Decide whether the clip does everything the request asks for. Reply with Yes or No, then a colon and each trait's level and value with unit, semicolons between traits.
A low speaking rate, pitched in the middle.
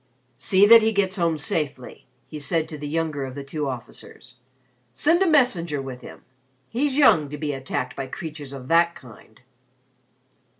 No: average, 170 wpm; medium, 155 Hz